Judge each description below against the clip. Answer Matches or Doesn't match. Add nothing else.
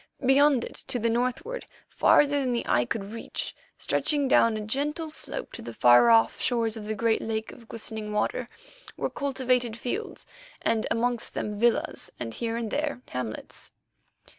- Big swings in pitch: Doesn't match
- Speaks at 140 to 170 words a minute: Matches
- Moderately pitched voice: Doesn't match